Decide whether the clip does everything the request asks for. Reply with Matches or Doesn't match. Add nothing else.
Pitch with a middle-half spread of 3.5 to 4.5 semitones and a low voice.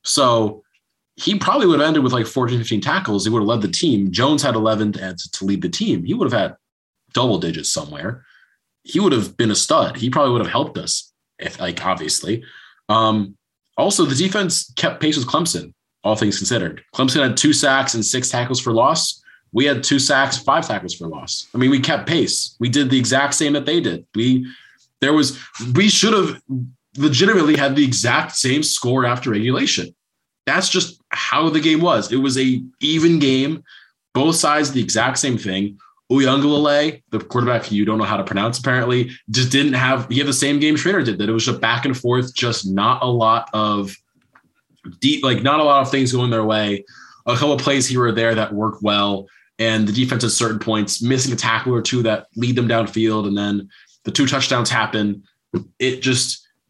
Matches